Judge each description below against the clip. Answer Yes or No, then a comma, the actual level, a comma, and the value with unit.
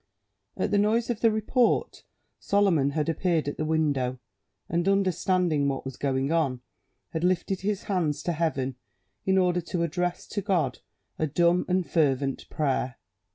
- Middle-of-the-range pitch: Yes, medium, 170 Hz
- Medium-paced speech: Yes, average, 155 wpm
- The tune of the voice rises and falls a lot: No, average, 4.7 semitones